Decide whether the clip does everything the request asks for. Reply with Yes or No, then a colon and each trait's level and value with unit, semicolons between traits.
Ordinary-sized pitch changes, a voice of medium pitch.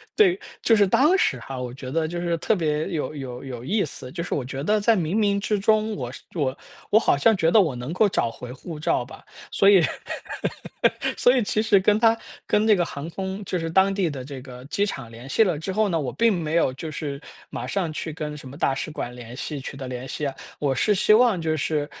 No: wide, 6.8 semitones; medium, 160 Hz